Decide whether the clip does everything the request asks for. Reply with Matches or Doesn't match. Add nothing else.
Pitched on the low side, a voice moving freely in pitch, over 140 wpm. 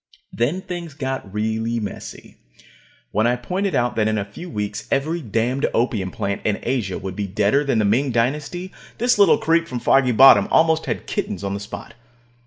Matches